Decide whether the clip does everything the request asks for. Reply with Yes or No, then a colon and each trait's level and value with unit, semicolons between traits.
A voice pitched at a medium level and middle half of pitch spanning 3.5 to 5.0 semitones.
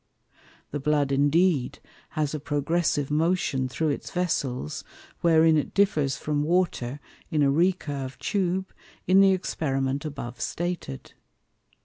Yes: medium, 150 Hz; average, 4.0 semitones